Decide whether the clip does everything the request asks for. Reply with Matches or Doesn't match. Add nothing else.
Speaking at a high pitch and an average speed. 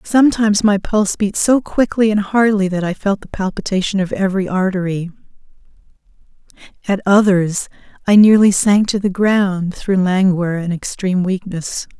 Matches